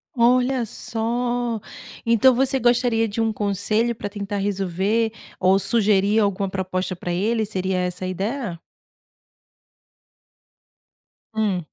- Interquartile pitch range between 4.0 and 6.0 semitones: No, average, 3.4 semitones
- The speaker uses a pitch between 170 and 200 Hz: No, high, 210 Hz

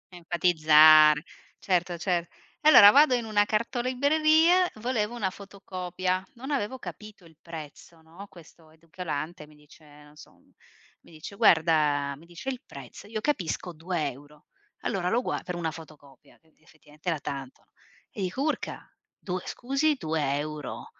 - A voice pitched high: No, medium, 175 Hz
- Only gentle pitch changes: No, wide, 5.5 semitones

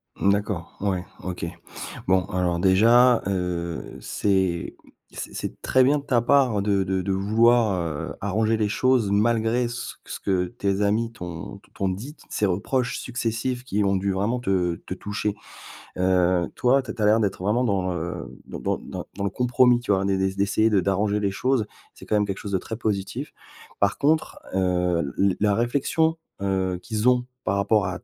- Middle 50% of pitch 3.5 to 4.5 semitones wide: Yes, average, 3.8 semitones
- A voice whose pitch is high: No, low, 100 Hz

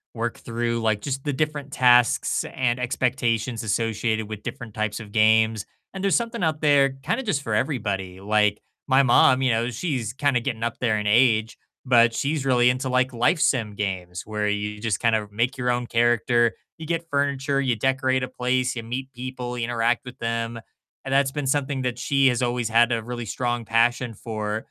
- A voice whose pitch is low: Yes, low, 120 Hz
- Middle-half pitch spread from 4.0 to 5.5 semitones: No, average, 2.8 semitones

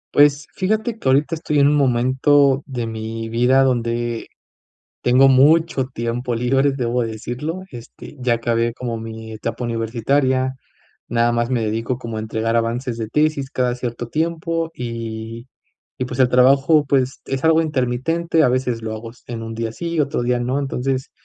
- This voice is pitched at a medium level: No, low, 125 Hz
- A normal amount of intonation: Yes, average, 3.1 semitones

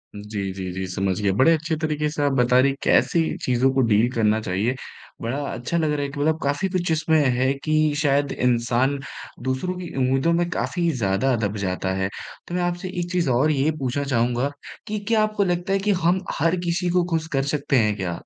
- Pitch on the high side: No, medium, 140 Hz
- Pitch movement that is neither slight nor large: No, wide, 5.9 semitones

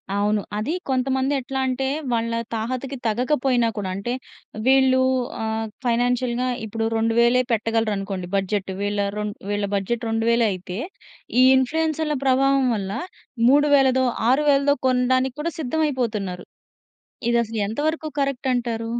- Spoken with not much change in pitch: No, average, 3.3 semitones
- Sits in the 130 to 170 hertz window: No, high, 245 Hz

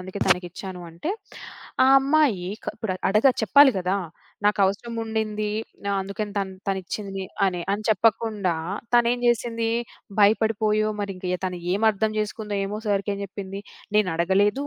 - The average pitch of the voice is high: Yes, high, 205 Hz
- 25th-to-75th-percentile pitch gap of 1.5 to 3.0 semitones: Yes, narrow, 2.6 semitones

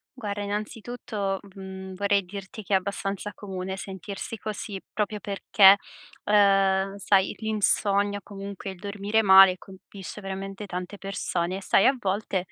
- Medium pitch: No, high, 195 Hz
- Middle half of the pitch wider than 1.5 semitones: No, narrow, 1.2 semitones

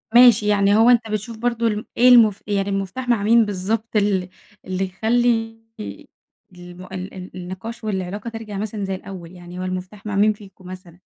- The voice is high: Yes, high, 205 Hz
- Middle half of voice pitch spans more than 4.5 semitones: No, average, 3.3 semitones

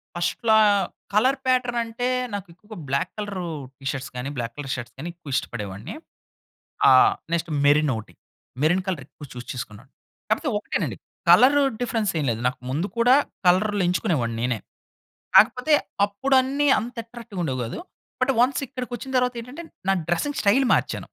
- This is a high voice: Yes, high, 200 Hz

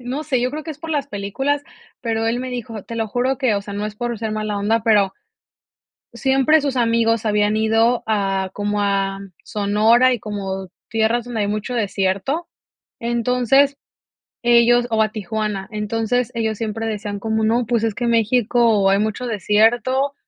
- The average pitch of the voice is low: No, high, 225 Hz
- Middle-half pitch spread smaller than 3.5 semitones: Yes, average, 2.8 semitones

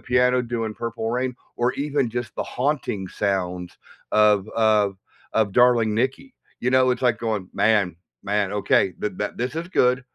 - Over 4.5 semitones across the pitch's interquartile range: No, average, 3.4 semitones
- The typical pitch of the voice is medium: No, low, 115 Hz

